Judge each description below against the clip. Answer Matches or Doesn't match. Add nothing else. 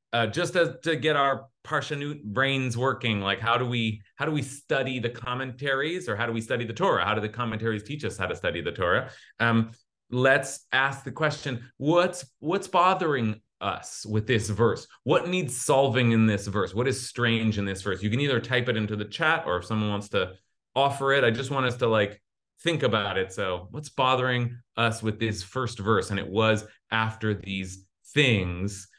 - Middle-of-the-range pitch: Doesn't match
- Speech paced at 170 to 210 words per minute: Matches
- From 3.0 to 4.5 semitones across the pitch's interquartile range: Matches